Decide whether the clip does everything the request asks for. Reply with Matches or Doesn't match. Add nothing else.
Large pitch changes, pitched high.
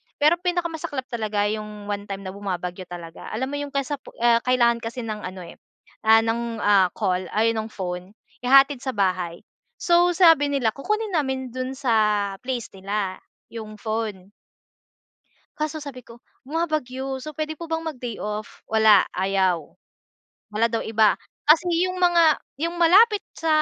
Matches